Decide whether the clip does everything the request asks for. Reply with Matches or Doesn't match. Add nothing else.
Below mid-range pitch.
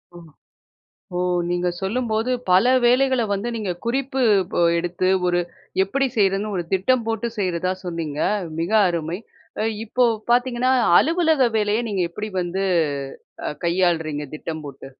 Doesn't match